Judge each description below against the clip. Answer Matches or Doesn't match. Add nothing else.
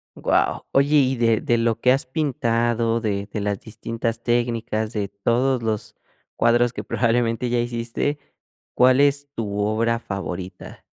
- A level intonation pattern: Matches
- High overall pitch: Doesn't match